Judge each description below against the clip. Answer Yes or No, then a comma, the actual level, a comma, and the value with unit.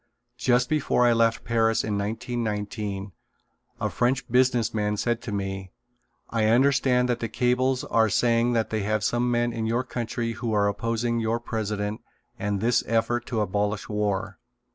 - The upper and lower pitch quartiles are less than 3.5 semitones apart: Yes, narrow, 2.5 semitones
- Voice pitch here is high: No, low, 115 Hz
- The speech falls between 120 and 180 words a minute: Yes, average, 165 wpm